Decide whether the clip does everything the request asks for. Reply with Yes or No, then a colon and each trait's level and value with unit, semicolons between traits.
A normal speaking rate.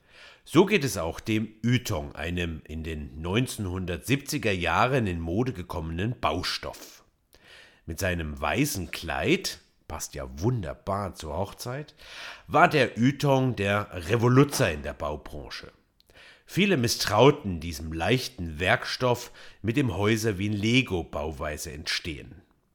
No: slow, 115 wpm